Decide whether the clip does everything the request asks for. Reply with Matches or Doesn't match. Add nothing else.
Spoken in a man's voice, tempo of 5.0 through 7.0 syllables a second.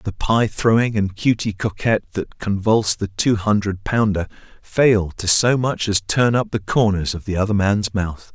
Doesn't match